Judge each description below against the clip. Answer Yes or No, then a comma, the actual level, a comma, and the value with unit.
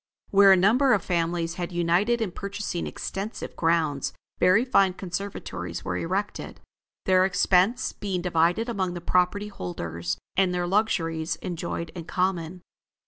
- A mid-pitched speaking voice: Yes, medium, 180 Hz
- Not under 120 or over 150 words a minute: Yes, average, 140 wpm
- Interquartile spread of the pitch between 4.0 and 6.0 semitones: No, average, 3.0 semitones